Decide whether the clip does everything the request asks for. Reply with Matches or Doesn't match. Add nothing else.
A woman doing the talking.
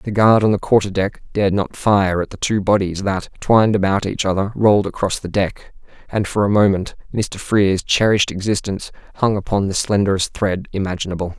Doesn't match